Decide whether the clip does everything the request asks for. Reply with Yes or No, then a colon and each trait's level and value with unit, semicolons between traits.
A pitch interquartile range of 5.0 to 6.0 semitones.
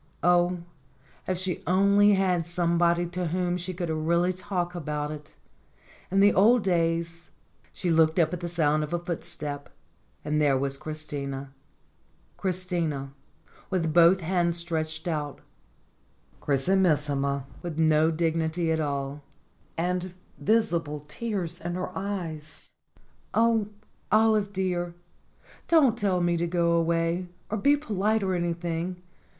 No: average, 2.7 semitones